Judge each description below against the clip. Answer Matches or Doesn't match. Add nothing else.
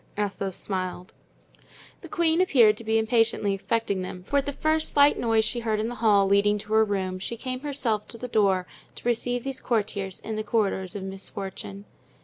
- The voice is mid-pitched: Doesn't match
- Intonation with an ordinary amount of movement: Matches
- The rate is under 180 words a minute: Doesn't match